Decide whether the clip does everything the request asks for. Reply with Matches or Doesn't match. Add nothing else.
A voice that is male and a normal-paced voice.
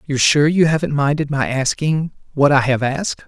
Matches